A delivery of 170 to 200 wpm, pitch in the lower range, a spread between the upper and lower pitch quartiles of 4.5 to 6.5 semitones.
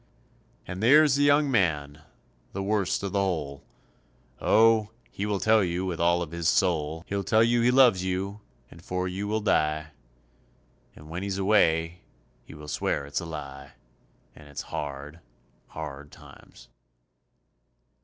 No: average, 155 wpm; very low, 90 Hz; average, 5.2 semitones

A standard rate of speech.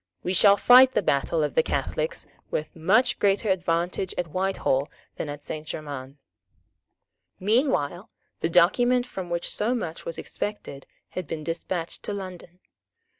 Yes: average, 145 wpm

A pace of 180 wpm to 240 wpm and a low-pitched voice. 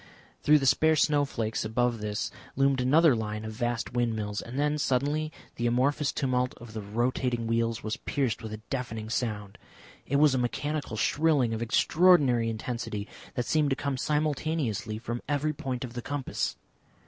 No: average, 165 wpm; low, 125 Hz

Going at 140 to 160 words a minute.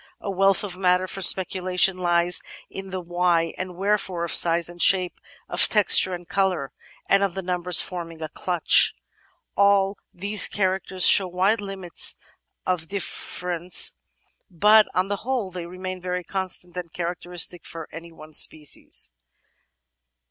Yes: average, 145 wpm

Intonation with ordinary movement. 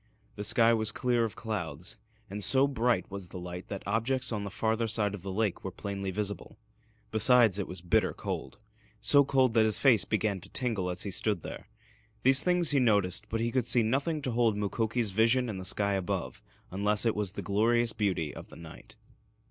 Yes: average, 3.3 semitones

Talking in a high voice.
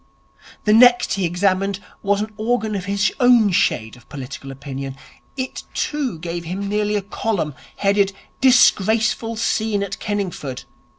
Yes: high, 200 Hz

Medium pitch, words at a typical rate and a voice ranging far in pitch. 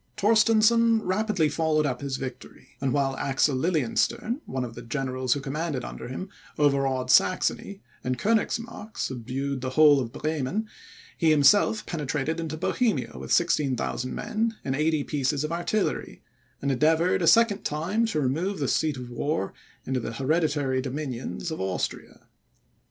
Yes: medium, 150 Hz; average, 150 wpm; wide, 5.7 semitones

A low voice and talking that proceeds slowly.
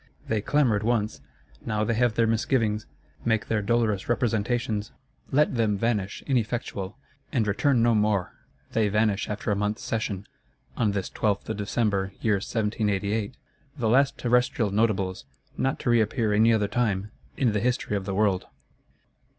No: low, 110 Hz; average, 150 wpm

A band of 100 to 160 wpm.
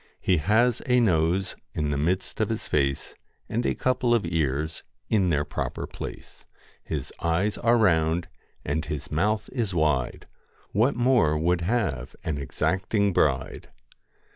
Yes: average, 145 wpm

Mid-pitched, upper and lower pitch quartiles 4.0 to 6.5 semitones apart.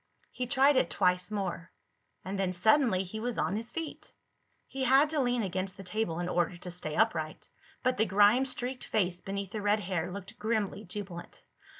No: high, 200 Hz; average, 4.9 semitones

